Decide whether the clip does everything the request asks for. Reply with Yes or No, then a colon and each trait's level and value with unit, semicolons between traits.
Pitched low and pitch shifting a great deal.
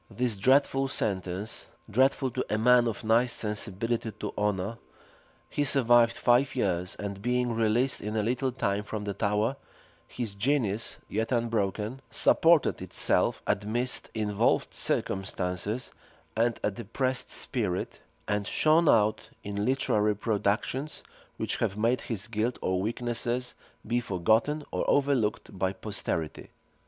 No: low, 110 Hz; average, 3.3 semitones